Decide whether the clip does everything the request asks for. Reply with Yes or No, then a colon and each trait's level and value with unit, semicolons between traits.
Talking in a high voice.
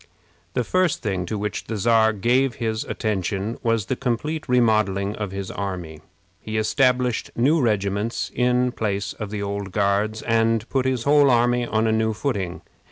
No: low, 110 Hz